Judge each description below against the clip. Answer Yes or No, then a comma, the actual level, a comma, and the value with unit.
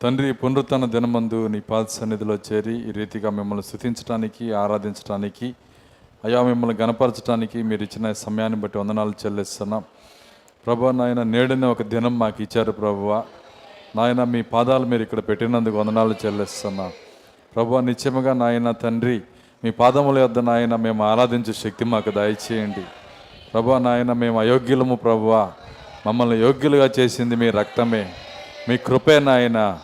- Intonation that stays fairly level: Yes, narrow, 2.3 semitones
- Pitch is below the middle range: Yes, low, 115 Hz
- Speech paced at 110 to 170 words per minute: Yes, fast, 125 wpm